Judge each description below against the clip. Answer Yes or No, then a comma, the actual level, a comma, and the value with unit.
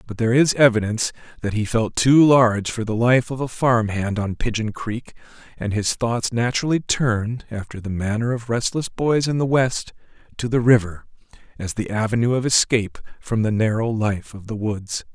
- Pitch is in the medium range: No, low, 115 Hz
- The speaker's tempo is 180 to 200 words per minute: Yes, average, 185 wpm